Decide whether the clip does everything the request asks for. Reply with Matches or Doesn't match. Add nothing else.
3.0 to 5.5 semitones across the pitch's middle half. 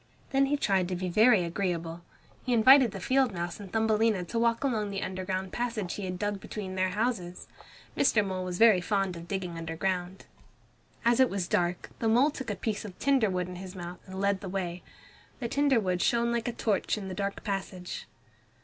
Matches